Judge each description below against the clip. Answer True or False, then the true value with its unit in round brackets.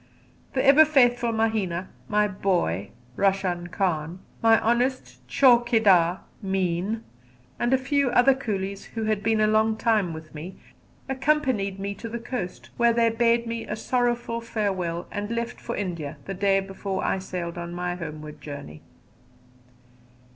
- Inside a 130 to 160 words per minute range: True (145 wpm)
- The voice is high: True (205 Hz)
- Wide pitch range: False (4.7 semitones)